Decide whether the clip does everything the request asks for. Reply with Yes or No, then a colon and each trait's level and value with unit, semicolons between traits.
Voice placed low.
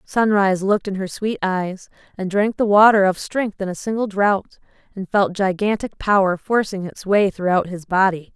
No: high, 195 Hz